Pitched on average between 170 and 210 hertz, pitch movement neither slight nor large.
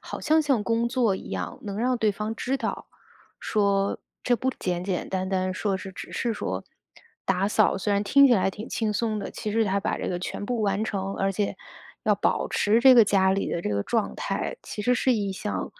Yes: high, 205 Hz; average, 3.1 semitones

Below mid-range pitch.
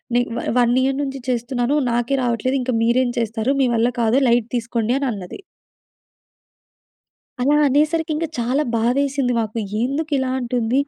No: high, 245 Hz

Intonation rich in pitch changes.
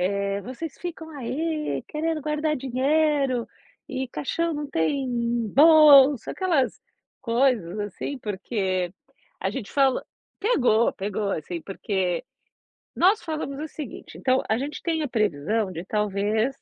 Yes: wide, 6.5 semitones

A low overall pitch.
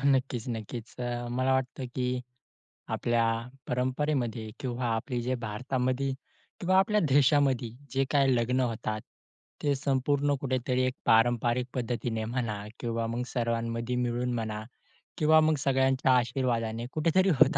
Yes: low, 125 Hz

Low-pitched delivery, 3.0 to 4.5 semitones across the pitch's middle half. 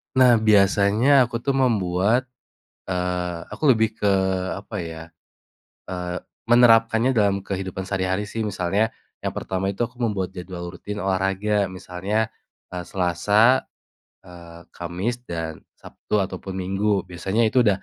Yes: low, 100 Hz; average, 3.6 semitones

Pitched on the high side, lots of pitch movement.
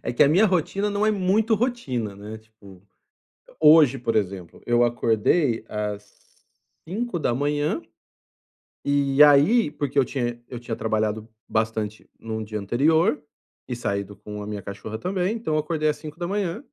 No: low, 130 Hz; wide, 7.3 semitones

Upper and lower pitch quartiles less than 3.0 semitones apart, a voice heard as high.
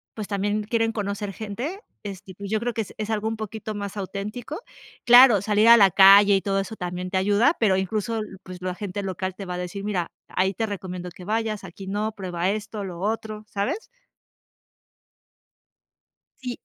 Yes: narrow, 2.4 semitones; high, 205 Hz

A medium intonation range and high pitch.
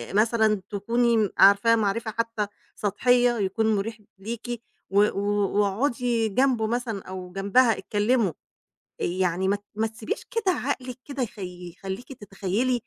Yes: average, 3.2 semitones; high, 215 Hz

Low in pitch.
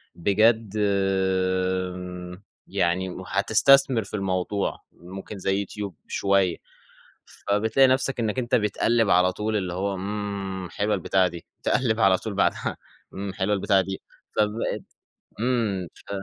Yes: low, 100 Hz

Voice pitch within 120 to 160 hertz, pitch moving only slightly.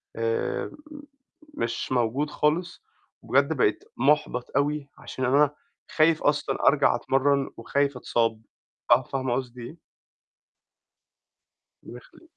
No: medium, 140 Hz; average, 3.3 semitones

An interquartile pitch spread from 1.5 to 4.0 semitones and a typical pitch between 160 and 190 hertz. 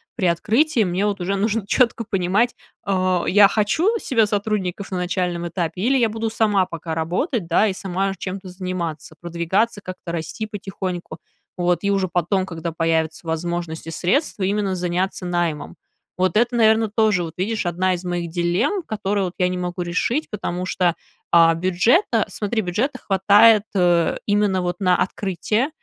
Yes: average, 3.2 semitones; medium, 185 Hz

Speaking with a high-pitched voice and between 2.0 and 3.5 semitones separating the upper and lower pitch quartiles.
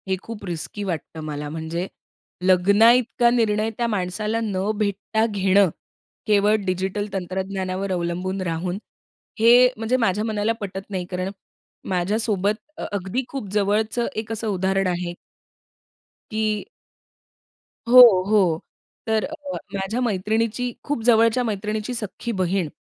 Yes: high, 205 Hz; average, 3.0 semitones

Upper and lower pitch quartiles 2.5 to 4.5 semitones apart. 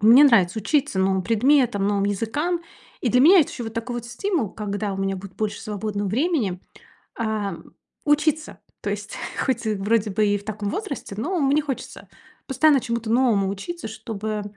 No: average, 5.2 semitones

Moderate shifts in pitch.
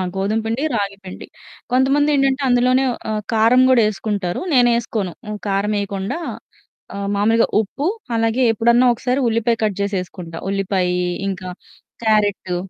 Yes: average, 3.5 semitones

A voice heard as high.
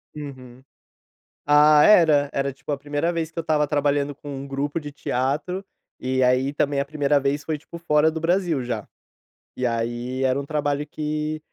No: medium, 145 Hz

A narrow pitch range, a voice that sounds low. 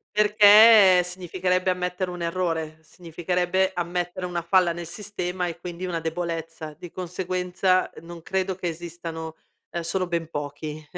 No: narrow, 1.7 semitones; medium, 175 Hz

